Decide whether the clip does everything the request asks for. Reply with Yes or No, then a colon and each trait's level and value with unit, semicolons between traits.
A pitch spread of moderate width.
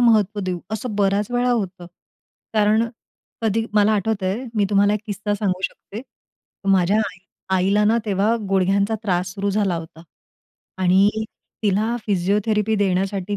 No: narrow, 2.1 semitones